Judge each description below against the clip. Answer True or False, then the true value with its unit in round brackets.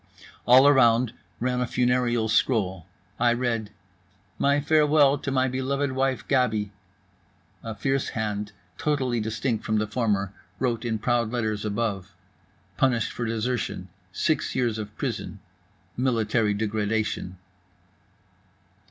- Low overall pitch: True (120 Hz)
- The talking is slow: True (115 wpm)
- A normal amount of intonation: True (3.3 semitones)